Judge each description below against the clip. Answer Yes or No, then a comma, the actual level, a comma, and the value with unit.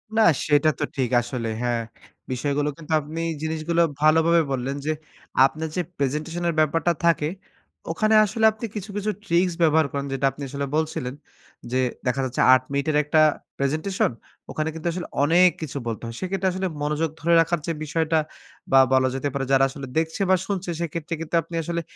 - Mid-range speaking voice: Yes, medium, 155 Hz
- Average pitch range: Yes, average, 3.3 semitones